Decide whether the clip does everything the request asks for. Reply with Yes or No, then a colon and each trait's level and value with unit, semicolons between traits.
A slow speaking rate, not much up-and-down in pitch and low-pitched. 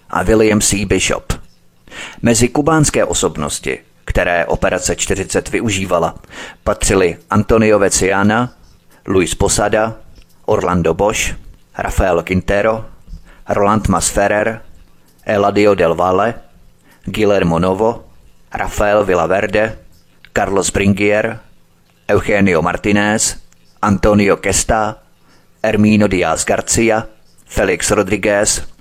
No: slow, 85 wpm; average, 3.0 semitones; low, 100 Hz